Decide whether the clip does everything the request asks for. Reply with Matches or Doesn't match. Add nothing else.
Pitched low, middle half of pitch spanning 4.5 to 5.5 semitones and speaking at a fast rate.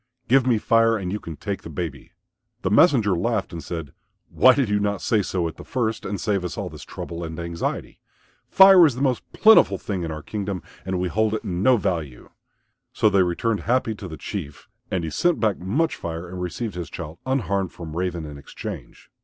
Matches